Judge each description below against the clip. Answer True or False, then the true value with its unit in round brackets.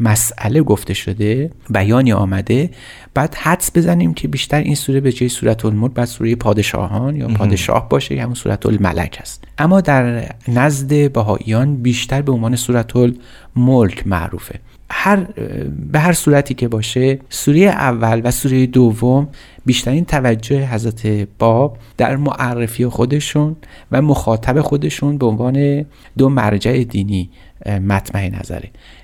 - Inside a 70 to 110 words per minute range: False (130 wpm)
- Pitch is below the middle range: True (120 Hz)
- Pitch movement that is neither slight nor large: True (4.3 semitones)